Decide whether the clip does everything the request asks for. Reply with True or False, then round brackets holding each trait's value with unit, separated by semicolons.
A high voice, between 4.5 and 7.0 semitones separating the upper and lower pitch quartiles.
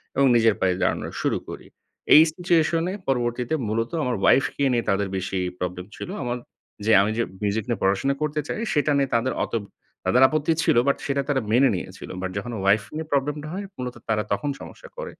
False (125 Hz; 5.5 semitones)